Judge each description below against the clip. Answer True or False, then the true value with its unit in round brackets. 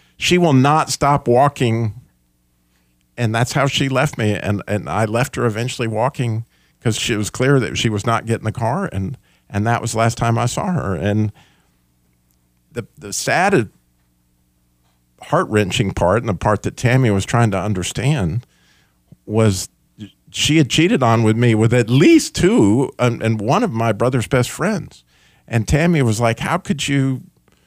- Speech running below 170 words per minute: False (175 wpm)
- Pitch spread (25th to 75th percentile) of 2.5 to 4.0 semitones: False (4.5 semitones)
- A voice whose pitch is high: False (115 Hz)